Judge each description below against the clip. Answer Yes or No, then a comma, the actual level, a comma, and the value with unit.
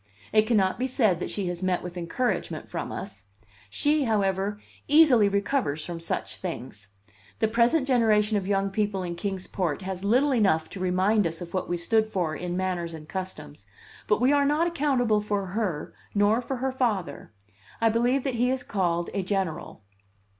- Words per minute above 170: Yes, average, 180 wpm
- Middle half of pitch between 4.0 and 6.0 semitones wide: Yes, average, 4.9 semitones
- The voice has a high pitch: Yes, high, 200 Hz